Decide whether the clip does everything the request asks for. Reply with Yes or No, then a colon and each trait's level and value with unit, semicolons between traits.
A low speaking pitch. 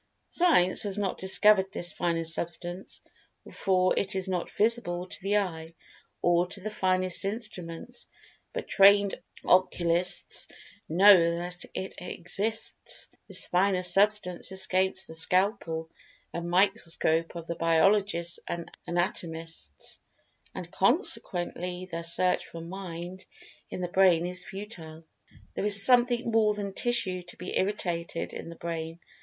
No: medium, 180 Hz